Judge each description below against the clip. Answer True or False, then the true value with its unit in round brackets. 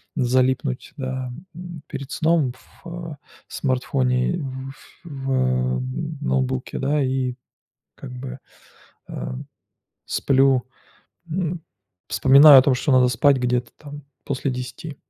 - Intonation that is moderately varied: False (2.3 semitones)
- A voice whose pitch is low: True (130 Hz)